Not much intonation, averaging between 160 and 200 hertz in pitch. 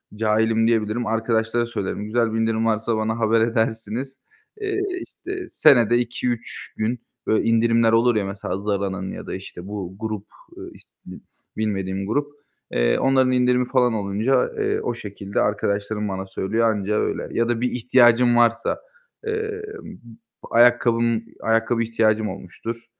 No: narrow, 2.2 semitones; low, 115 Hz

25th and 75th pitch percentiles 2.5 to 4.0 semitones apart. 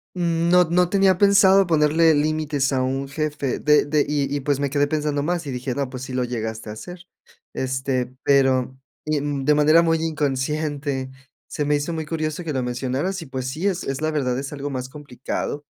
Yes: average, 3.2 semitones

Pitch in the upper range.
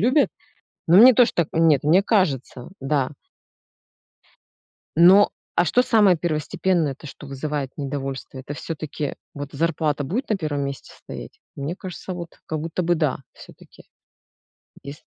No: medium, 155 Hz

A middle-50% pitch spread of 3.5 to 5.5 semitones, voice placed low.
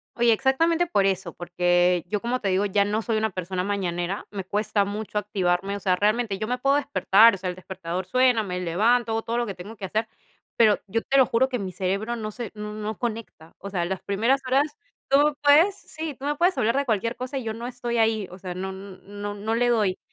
No: average, 4.1 semitones; high, 215 Hz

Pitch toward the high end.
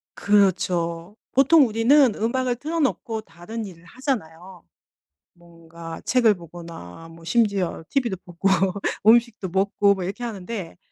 Yes: high, 195 Hz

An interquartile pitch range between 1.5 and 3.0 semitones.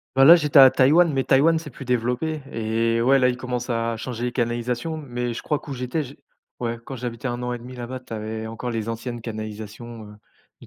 Yes: narrow, 2.5 semitones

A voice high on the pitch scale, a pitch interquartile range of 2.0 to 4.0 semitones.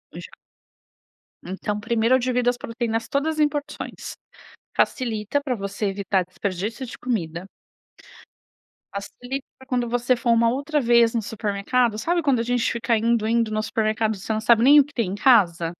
Yes: high, 230 Hz; average, 2.9 semitones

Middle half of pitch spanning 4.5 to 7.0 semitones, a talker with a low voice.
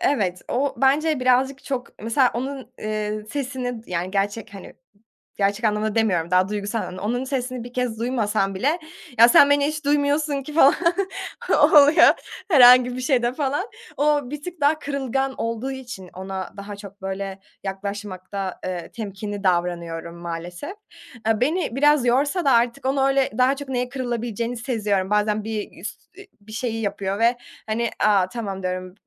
No: average, 5.2 semitones; high, 235 Hz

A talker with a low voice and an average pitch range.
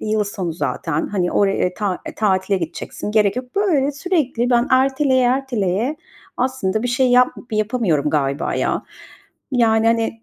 No: high, 225 Hz; average, 5.0 semitones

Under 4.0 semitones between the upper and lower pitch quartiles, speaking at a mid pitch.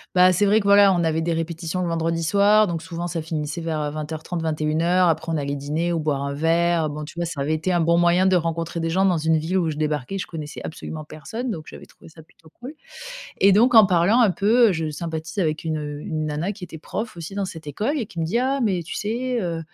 Yes: average, 3.2 semitones; medium, 165 Hz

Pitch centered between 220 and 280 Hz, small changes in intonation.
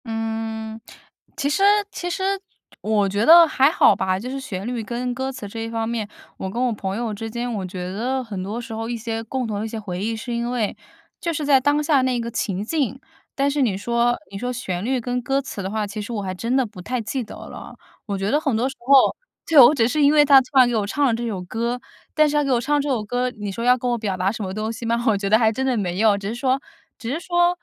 No: high, 235 Hz; average, 3.7 semitones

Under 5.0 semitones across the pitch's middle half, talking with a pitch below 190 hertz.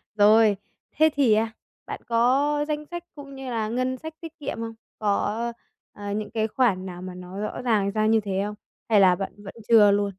No: average, 4.1 semitones; high, 220 Hz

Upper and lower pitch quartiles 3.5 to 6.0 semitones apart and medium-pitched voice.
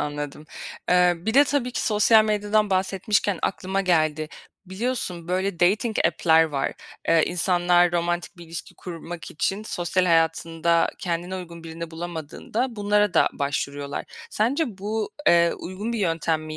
Yes: average, 3.9 semitones; medium, 175 Hz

